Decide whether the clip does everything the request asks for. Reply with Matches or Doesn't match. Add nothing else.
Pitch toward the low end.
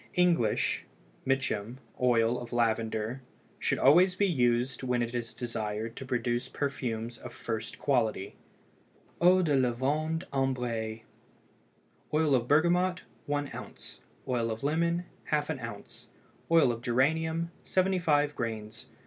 Matches